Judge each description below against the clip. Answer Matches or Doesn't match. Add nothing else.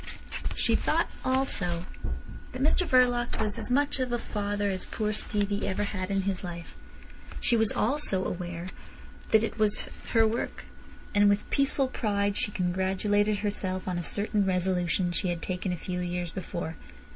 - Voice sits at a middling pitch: Doesn't match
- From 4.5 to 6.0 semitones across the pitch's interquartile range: Doesn't match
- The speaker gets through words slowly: Doesn't match